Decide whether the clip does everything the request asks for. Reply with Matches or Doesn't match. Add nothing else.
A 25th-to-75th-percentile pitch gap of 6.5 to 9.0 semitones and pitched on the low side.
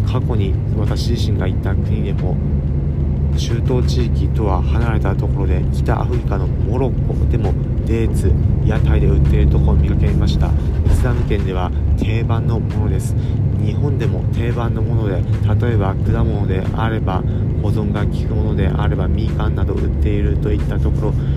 Matches